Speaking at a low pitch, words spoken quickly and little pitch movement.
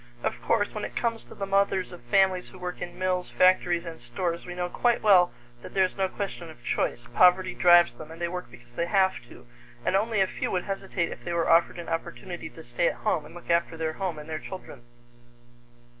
No: medium, 175 Hz; fast, 235 wpm; narrow, 2.3 semitones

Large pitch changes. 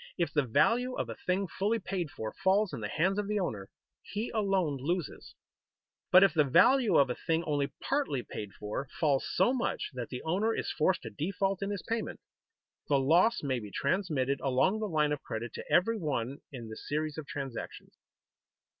Yes: wide, 6.4 semitones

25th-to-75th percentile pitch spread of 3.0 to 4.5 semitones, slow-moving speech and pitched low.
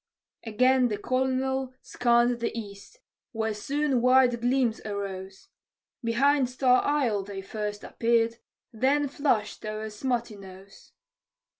No: average, 3.6 semitones; slow, 110 wpm; high, 235 Hz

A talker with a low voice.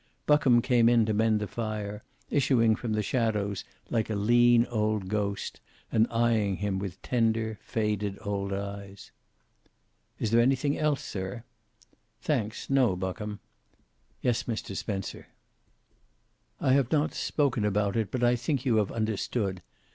Yes: low, 110 Hz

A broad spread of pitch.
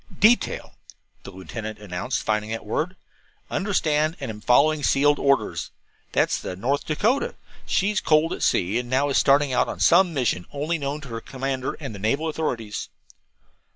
Yes: wide, 5.7 semitones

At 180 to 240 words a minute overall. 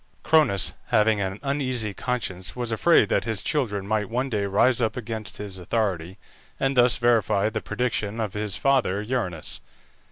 No: average, 160 wpm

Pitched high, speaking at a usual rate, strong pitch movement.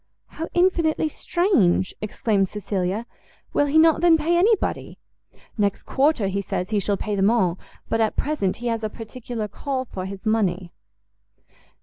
Yes: high, 225 Hz; average, 155 wpm; wide, 7.6 semitones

